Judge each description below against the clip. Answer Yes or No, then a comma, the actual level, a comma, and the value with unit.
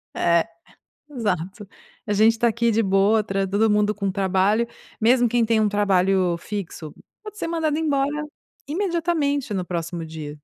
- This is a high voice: Yes, high, 210 Hz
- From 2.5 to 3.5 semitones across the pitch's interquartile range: No, average, 4.2 semitones